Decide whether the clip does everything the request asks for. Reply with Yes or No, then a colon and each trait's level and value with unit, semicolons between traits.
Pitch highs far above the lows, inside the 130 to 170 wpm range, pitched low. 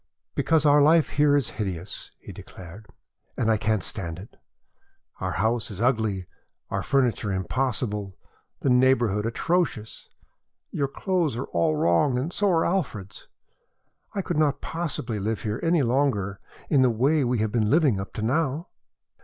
Yes: wide, 5.8 semitones; average, 155 wpm; low, 120 Hz